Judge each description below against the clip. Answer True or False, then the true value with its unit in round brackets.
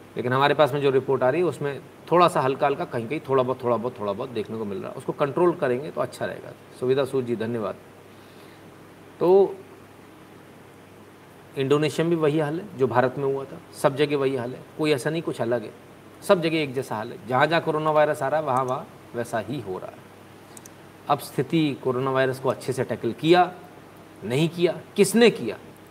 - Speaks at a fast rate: True (215 wpm)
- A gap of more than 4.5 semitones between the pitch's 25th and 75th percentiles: False (3.7 semitones)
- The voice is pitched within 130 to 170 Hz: True (140 Hz)